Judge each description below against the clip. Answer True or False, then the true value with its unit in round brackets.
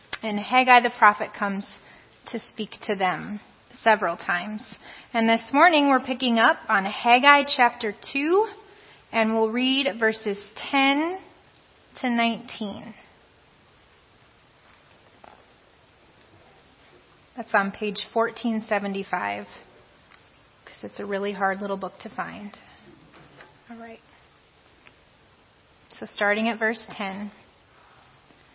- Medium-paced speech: False (100 wpm)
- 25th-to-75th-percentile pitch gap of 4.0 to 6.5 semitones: False (3.2 semitones)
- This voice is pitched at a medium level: False (220 Hz)